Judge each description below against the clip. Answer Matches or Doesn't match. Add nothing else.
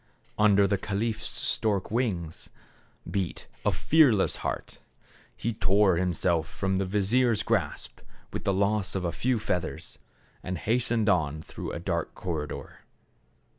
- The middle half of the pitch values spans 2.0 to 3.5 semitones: Matches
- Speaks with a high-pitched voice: Doesn't match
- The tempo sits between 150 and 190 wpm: Doesn't match